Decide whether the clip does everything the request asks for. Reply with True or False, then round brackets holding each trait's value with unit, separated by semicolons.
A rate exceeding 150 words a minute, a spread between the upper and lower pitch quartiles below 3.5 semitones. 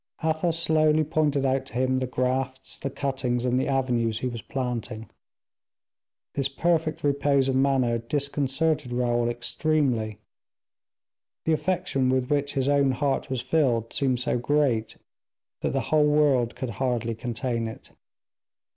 False (140 wpm; 3.0 semitones)